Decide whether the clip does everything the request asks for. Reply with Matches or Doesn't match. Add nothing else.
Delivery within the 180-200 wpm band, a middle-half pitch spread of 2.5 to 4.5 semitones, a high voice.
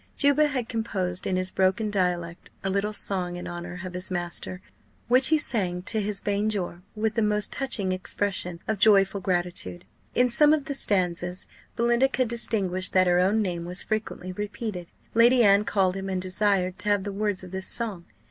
Matches